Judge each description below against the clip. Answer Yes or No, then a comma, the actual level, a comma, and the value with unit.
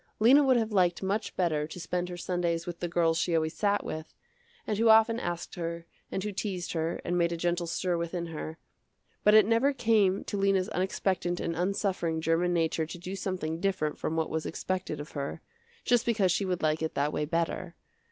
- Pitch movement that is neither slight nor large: Yes, average, 3.1 semitones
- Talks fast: Yes, fast, 210 wpm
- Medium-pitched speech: Yes, medium, 175 Hz